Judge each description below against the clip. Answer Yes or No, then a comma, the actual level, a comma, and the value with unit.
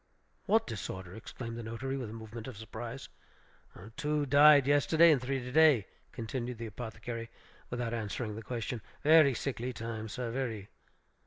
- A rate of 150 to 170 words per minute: Yes, average, 155 wpm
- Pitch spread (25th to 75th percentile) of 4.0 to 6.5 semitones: No, average, 3.4 semitones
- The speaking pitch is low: Yes, low, 120 Hz